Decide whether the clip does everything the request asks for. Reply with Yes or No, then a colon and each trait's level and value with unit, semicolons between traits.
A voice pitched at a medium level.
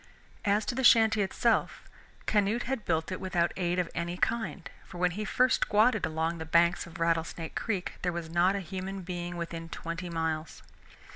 Yes: medium, 180 Hz